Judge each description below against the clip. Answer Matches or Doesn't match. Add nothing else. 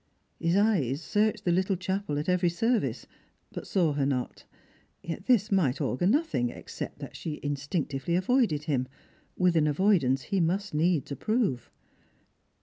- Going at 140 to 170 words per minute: Matches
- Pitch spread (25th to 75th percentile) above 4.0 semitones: Matches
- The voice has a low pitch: Doesn't match